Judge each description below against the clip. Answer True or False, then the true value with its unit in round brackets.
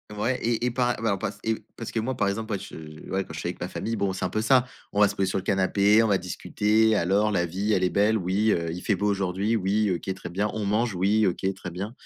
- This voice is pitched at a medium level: False (100 Hz)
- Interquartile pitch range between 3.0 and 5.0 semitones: False (2.6 semitones)